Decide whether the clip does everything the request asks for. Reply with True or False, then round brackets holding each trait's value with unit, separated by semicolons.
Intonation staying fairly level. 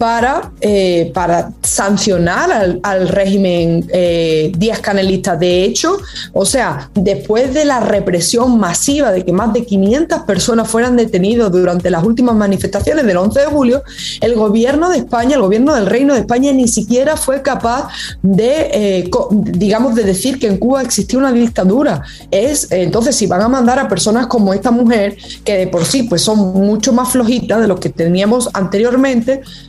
False (4.7 semitones)